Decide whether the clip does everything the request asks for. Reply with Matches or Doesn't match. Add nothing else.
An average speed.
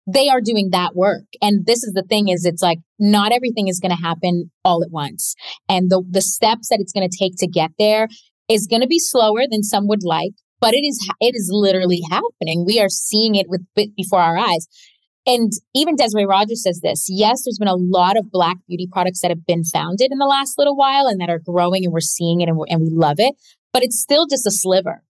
Doesn't match